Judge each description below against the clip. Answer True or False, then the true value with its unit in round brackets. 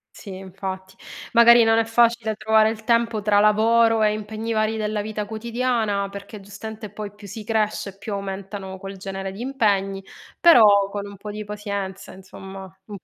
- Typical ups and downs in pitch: False (2.0 semitones)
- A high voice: True (210 Hz)